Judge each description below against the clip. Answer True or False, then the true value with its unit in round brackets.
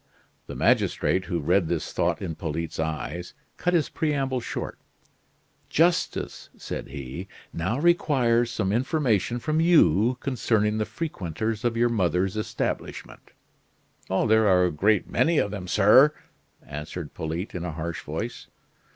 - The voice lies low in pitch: True (105 Hz)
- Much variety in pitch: True (6.2 semitones)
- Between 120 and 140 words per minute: True (135 wpm)